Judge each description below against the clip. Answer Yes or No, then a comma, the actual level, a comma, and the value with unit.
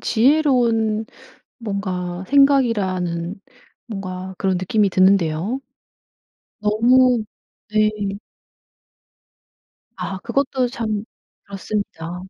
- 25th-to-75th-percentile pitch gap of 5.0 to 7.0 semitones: No, average, 4.3 semitones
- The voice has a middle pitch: No, high, 210 Hz